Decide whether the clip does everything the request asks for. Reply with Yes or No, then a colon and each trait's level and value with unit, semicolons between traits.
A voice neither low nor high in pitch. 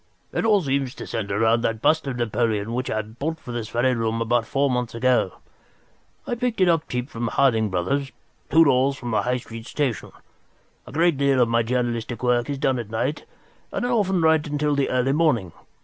No: low, 125 Hz